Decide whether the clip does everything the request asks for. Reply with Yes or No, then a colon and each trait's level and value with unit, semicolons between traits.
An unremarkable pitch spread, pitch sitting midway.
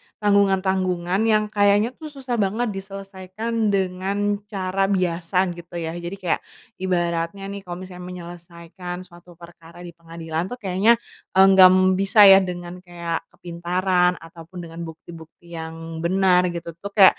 No: narrow, 2.3 semitones; medium, 180 Hz